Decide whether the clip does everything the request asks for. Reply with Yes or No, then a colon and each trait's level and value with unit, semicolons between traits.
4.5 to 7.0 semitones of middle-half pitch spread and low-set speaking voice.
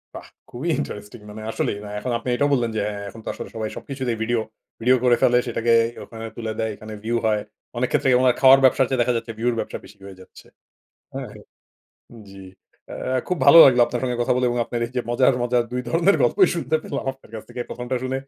No: narrow, 2.4 semitones; low, 120 Hz